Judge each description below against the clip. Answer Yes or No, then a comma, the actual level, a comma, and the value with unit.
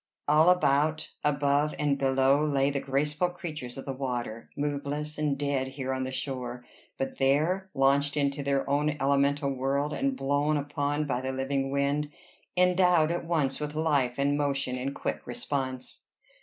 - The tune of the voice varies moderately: No, narrow, 1.9 semitones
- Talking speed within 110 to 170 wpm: Yes, average, 160 wpm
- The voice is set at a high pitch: No, medium, 140 Hz